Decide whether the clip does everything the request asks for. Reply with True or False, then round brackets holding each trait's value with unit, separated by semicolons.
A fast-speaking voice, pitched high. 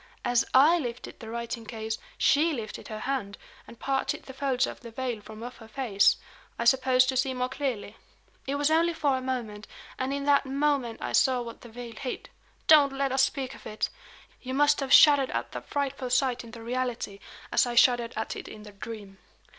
True (210 wpm; 255 Hz)